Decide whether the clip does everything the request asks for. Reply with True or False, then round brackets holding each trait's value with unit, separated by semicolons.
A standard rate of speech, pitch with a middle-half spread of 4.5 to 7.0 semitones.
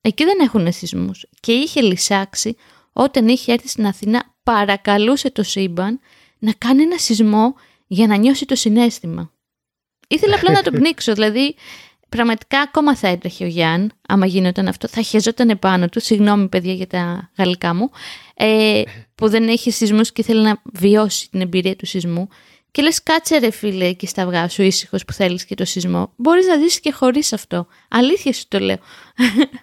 False (175 wpm; 5.1 semitones)